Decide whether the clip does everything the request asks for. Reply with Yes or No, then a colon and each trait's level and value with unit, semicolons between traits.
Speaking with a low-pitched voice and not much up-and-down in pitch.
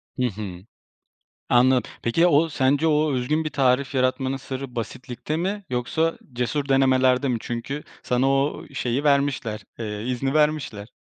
No: low, 130 Hz; average, 3.1 semitones